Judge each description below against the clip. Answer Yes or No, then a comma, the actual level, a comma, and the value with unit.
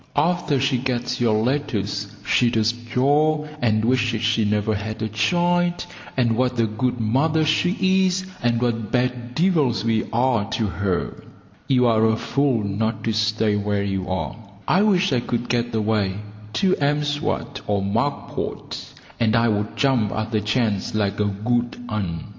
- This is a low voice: Yes, low, 115 Hz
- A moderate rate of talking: Yes, average, 165 wpm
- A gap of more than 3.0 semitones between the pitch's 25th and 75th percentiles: Yes, average, 3.9 semitones